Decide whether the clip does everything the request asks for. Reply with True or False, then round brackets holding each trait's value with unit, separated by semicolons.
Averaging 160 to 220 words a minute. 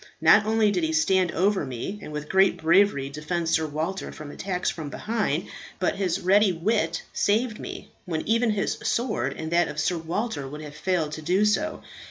True (195 wpm)